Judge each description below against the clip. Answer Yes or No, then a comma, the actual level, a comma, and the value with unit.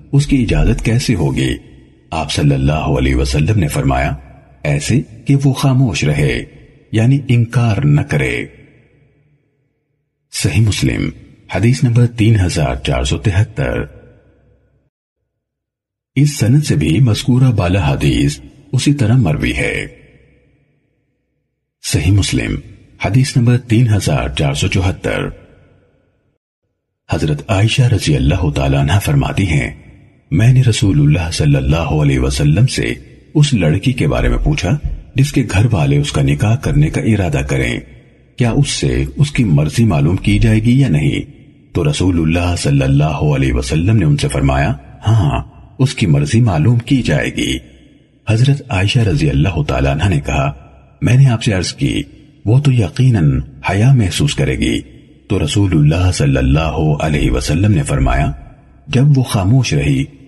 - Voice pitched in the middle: No, low, 120 Hz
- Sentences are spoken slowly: No, average, 150 wpm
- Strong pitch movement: Yes, wide, 6.6 semitones